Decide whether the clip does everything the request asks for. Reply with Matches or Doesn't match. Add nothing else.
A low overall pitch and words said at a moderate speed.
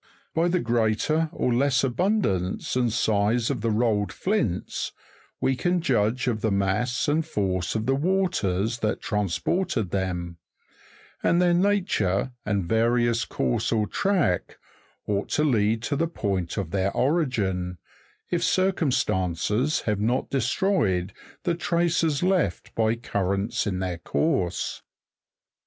Doesn't match